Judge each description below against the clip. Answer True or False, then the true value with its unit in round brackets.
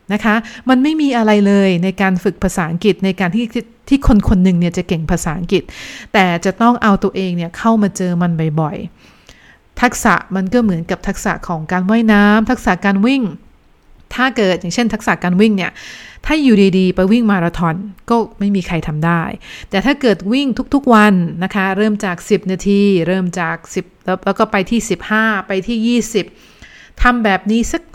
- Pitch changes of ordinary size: True (3.3 semitones)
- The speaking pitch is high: True (200 Hz)